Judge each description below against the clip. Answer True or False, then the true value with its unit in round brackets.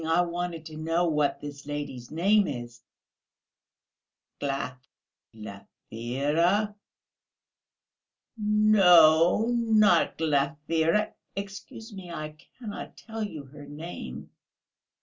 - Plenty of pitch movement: True (5.8 semitones)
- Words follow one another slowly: True (90 wpm)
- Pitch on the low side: False (160 Hz)